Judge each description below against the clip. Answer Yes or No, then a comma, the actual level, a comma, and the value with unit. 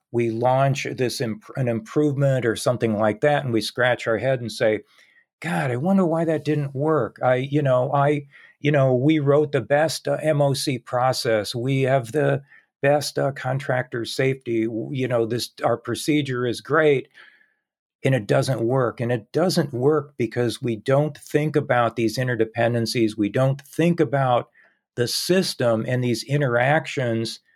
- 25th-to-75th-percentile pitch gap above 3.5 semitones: Yes, average, 3.9 semitones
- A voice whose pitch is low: Yes, low, 130 Hz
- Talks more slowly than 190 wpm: Yes, average, 165 wpm